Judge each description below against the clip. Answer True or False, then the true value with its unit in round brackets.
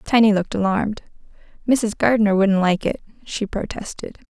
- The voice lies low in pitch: False (210 Hz)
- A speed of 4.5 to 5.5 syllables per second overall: False (6.0 syllables/s)